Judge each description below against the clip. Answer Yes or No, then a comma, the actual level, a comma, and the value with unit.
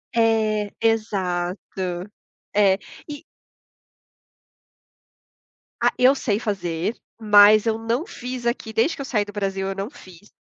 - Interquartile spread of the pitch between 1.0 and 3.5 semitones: Yes, average, 2.8 semitones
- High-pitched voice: Yes, high, 215 Hz